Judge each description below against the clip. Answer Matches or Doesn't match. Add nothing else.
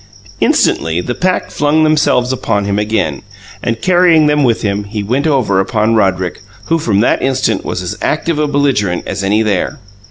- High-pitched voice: Doesn't match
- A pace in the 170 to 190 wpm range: Matches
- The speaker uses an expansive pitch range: Matches